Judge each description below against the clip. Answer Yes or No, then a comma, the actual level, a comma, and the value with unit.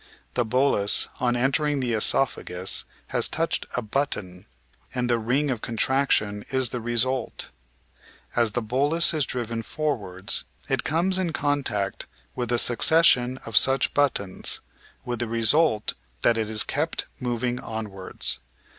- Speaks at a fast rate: No, average, 145 wpm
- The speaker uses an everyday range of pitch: Yes, average, 3.9 semitones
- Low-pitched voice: Yes, low, 120 Hz